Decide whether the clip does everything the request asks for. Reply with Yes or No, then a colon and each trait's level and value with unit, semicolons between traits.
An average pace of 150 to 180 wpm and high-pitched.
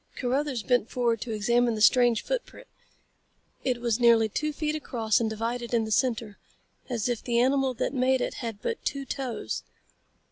Yes: average, 175 wpm; high, 240 Hz